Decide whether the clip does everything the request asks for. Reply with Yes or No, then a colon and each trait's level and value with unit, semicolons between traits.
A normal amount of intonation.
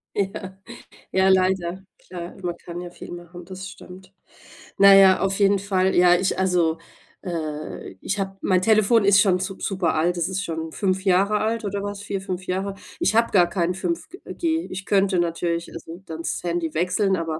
No: narrow, 2.2 semitones